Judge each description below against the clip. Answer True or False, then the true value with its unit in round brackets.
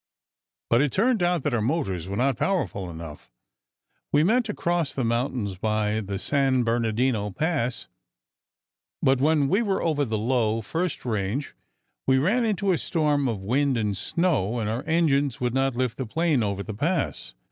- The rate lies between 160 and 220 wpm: True (175 wpm)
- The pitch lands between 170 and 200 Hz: False (130 Hz)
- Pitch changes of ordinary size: False (6.7 semitones)